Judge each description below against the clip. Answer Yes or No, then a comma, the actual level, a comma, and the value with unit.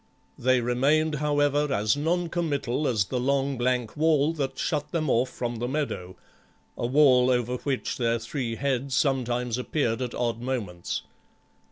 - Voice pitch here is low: Yes, low, 130 Hz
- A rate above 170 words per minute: No, average, 155 wpm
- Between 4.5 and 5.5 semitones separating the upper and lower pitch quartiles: No, average, 3.3 semitones